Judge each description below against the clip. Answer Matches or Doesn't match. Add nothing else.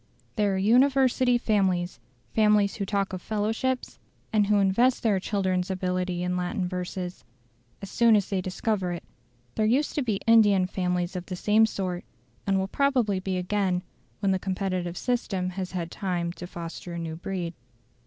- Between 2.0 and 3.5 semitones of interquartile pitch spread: Matches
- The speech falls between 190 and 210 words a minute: Doesn't match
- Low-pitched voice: Doesn't match